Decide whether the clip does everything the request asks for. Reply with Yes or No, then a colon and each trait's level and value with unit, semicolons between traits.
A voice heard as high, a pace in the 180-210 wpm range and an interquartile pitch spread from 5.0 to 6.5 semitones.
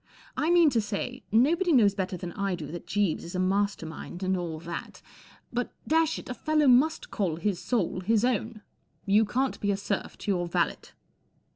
Yes: high, 205 Hz; average, 200 wpm; wide, 5.4 semitones